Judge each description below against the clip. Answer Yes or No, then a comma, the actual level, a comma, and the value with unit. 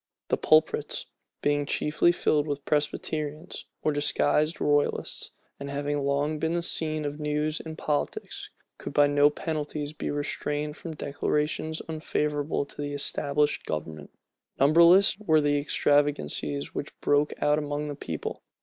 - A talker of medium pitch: Yes, medium, 150 Hz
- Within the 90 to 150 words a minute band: Yes, average, 140 wpm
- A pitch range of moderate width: No, narrow, 1.1 semitones